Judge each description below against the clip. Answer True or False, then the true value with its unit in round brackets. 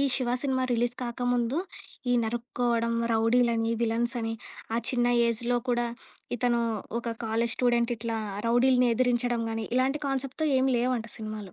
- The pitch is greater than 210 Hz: True (240 Hz)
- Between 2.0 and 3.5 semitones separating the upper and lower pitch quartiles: False (1.3 semitones)